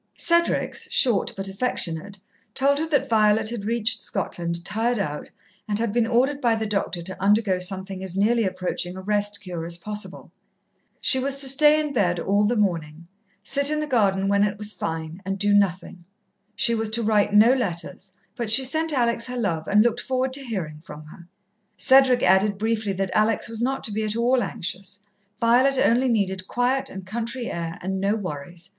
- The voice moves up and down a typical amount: Yes, average, 4.2 semitones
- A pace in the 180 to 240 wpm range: Yes, average, 190 wpm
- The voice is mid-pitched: No, high, 210 Hz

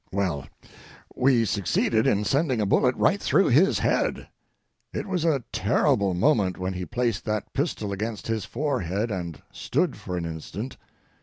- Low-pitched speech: Yes, low, 110 Hz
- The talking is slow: No, average, 155 wpm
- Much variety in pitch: Yes, wide, 5.8 semitones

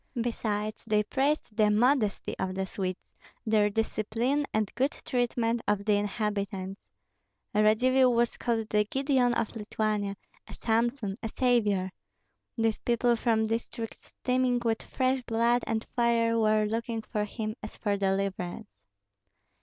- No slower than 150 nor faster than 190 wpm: No, slow, 135 wpm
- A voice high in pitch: Yes, high, 225 Hz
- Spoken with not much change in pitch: Yes, narrow, 2.3 semitones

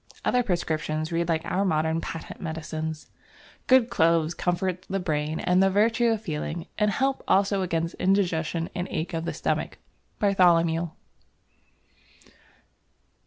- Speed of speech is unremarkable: No, slow, 130 wpm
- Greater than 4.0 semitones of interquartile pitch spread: No, average, 3.3 semitones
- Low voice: No, medium, 170 Hz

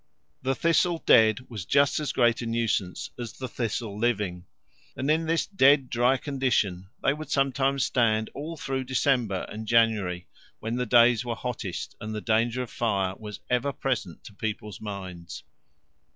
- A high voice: No, low, 120 Hz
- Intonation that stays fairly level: No, average, 3.9 semitones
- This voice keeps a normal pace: Yes, average, 165 wpm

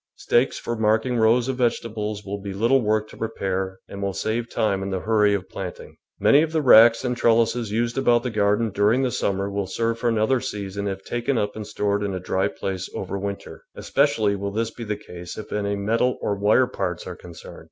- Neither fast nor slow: No, fast, 220 wpm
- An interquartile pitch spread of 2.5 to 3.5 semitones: Yes, average, 2.9 semitones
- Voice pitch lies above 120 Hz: No, low, 105 Hz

